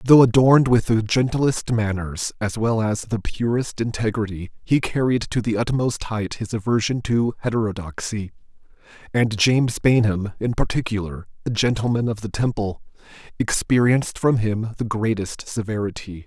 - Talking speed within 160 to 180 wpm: No, average, 140 wpm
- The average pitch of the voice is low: Yes, low, 115 Hz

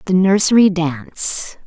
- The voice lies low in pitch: No, medium, 180 Hz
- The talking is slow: Yes, slow, 110 wpm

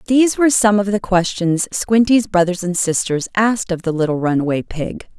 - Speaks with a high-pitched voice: Yes, high, 195 Hz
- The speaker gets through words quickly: No, average, 185 wpm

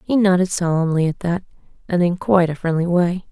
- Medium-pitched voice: Yes, medium, 175 Hz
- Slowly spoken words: No, average, 200 wpm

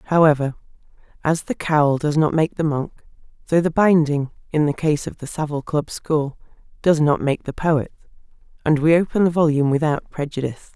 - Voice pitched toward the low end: No, medium, 155 Hz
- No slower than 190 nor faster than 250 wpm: No, average, 180 wpm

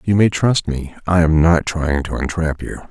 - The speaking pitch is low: Yes, very low, 85 Hz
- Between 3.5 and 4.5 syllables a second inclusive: Yes, 4.4 syllables/s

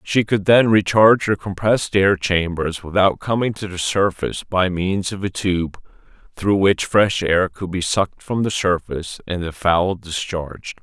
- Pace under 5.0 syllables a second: Yes, 4.5 syllables/s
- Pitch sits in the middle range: No, very low, 95 Hz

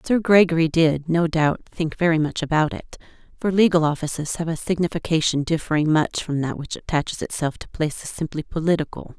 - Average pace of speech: Yes, average, 175 wpm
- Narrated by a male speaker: No, female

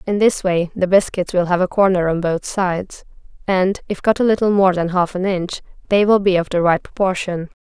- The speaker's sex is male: No, female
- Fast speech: Yes, fast, 230 wpm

